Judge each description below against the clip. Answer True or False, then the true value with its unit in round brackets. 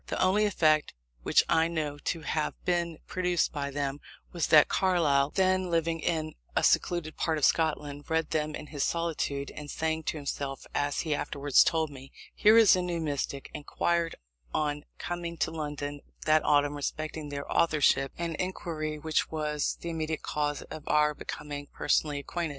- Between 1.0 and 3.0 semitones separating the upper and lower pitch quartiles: True (2.5 semitones)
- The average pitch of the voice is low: False (155 Hz)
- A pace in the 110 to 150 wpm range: False (170 wpm)